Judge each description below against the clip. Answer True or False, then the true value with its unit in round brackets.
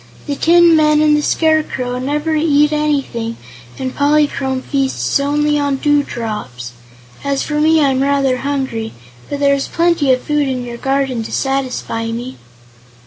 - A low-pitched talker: False (280 Hz)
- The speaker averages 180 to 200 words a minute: False (150 wpm)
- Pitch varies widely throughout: False (2.6 semitones)